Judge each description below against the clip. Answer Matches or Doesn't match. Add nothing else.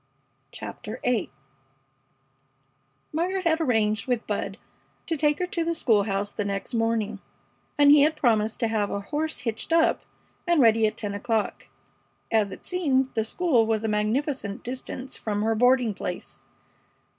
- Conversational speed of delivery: Matches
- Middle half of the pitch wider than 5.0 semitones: Matches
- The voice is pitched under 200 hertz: Doesn't match